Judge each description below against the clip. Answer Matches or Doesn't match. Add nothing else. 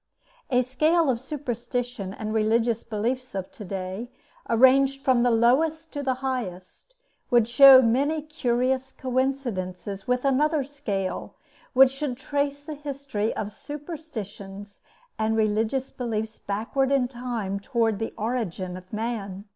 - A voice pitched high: Matches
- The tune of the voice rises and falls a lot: Doesn't match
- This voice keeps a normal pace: Doesn't match